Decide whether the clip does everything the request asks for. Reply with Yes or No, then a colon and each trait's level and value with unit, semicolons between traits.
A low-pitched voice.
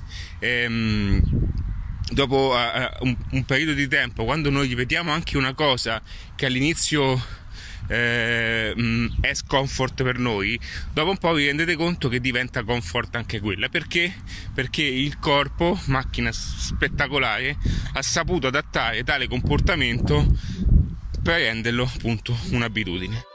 Yes: low, 120 Hz